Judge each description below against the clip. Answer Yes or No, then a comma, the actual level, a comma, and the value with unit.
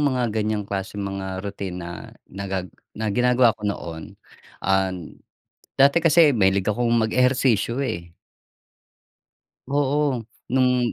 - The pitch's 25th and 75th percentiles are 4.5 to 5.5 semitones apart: Yes, average, 4.8 semitones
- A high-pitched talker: No, low, 110 Hz